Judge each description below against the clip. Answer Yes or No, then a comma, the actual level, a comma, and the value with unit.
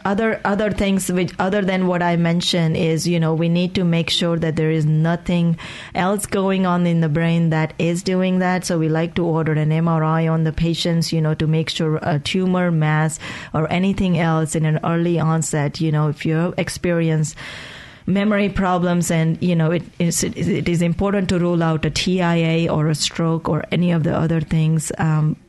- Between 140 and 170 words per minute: No, average, 200 wpm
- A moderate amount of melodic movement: No, narrow, 2.2 semitones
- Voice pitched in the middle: Yes, medium, 170 Hz